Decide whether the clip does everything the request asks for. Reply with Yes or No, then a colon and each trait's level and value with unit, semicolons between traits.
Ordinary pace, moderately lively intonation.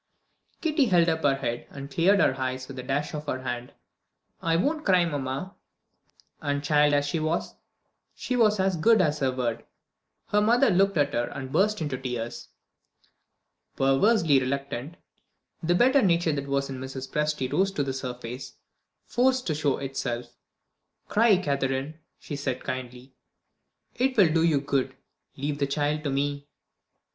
Yes: average, 160 wpm; average, 4.8 semitones